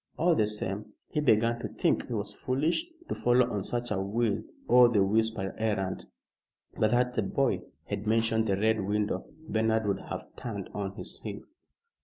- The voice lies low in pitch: Yes, low, 110 Hz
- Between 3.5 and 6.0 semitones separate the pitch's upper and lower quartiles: No, average, 2.8 semitones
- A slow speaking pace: No, average, 180 wpm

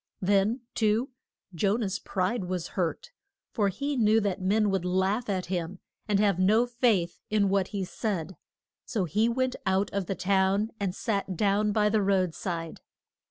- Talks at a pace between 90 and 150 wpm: No, average, 170 wpm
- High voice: Yes, high, 200 Hz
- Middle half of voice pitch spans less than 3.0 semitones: Yes, narrow, 2.5 semitones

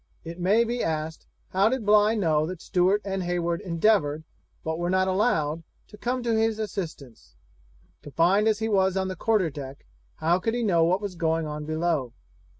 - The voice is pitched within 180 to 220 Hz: Yes, medium, 185 Hz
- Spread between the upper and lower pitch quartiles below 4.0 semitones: No, average, 4.6 semitones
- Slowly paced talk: No, average, 185 wpm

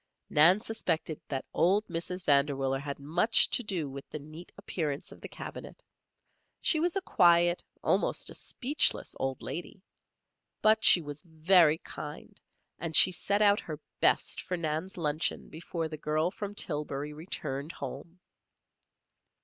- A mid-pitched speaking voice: Yes, medium, 165 Hz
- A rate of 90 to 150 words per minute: Yes, average, 145 wpm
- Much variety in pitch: No, average, 3.9 semitones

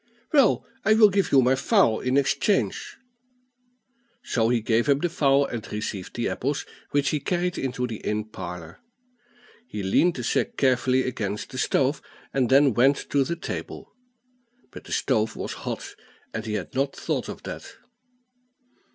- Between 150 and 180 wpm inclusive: Yes, average, 165 wpm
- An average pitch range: Yes, average, 4.3 semitones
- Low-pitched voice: Yes, low, 130 Hz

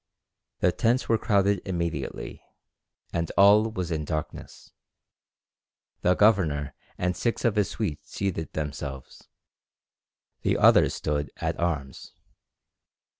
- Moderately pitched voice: No, very low, 85 Hz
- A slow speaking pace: Yes, slow, 110 wpm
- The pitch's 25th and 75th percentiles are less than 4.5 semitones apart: No, average, 5.2 semitones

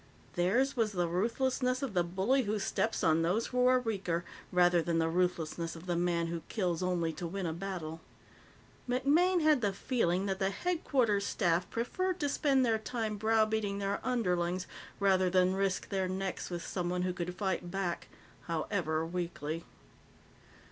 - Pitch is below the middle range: No, high, 190 Hz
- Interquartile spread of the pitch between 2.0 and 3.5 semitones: No, average, 4.5 semitones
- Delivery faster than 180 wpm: No, average, 165 wpm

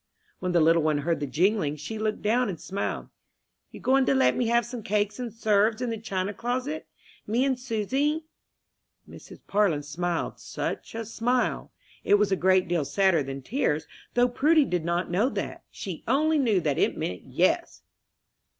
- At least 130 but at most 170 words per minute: No, average, 180 wpm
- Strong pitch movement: Yes, wide, 6.2 semitones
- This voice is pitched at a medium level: No, high, 210 Hz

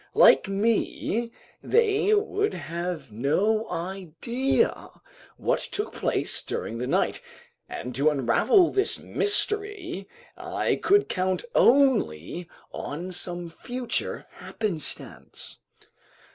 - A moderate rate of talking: No, slow, 95 wpm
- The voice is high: Yes, high, 195 Hz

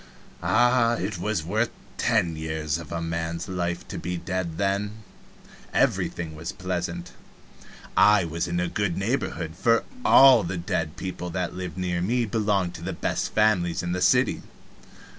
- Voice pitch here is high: No, very low, 90 Hz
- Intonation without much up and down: No, average, 3.5 semitones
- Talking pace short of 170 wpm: Yes, average, 160 wpm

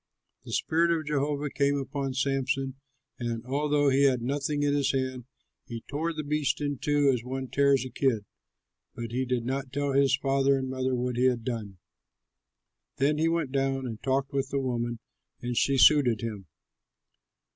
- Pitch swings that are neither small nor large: No, narrow, 2.2 semitones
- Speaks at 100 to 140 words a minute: No, average, 180 wpm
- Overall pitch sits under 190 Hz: Yes, low, 135 Hz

